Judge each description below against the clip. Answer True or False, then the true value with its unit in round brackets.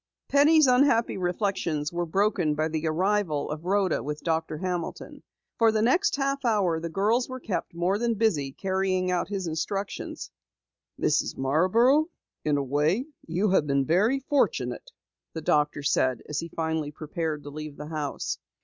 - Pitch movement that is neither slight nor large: False (5.8 semitones)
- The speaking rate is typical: True (160 wpm)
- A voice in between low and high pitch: True (175 Hz)